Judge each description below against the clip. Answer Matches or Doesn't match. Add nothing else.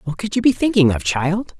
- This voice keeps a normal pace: Doesn't match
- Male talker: Doesn't match